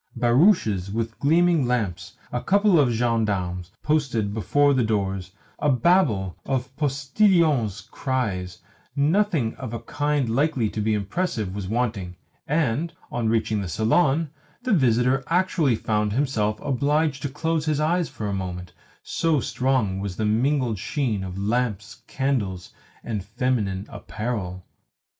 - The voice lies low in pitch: Yes, low, 120 Hz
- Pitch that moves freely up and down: Yes, wide, 5.9 semitones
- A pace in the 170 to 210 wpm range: No, slow, 135 wpm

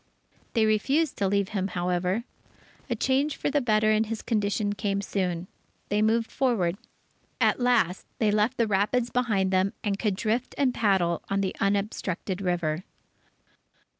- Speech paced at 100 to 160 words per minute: Yes, average, 155 wpm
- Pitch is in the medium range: No, high, 205 Hz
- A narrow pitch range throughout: No, average, 3.3 semitones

